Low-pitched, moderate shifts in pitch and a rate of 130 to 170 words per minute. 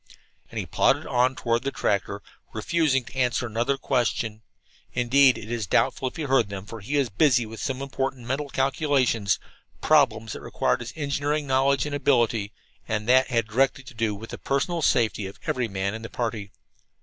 No: low, 125 Hz; average, 3.5 semitones; average, 185 wpm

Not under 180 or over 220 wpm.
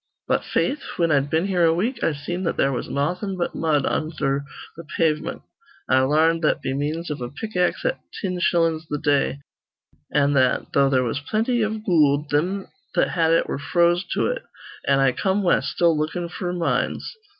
Yes: average, 195 wpm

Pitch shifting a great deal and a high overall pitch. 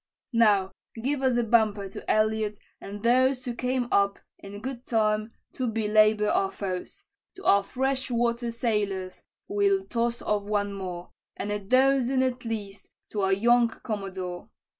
No: average, 3.6 semitones; high, 220 Hz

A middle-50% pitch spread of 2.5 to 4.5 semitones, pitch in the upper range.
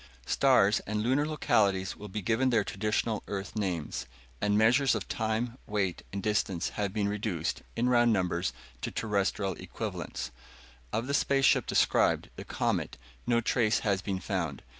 No: average, 3.2 semitones; low, 105 Hz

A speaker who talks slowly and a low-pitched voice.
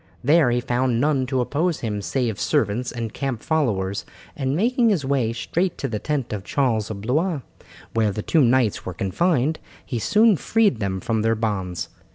No: average, 185 wpm; low, 125 Hz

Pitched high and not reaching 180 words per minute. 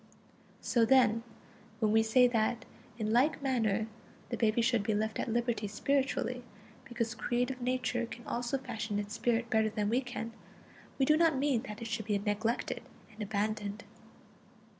Yes: high, 230 Hz; average, 160 wpm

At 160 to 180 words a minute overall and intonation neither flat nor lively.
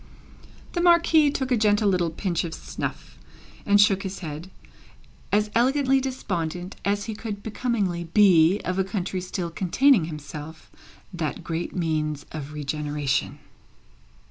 No: slow, 135 wpm; average, 4.9 semitones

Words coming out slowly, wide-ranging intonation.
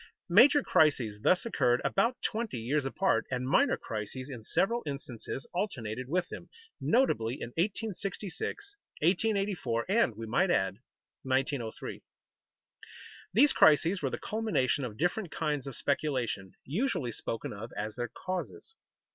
Yes: slow, 130 wpm; wide, 8.5 semitones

